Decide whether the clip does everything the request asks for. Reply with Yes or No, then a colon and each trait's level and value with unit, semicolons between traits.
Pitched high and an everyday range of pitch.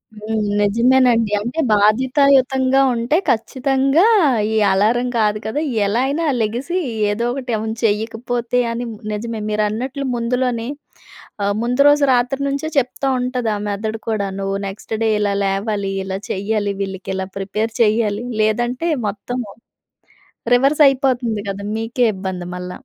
Yes: high, 230 Hz; average, 3.5 semitones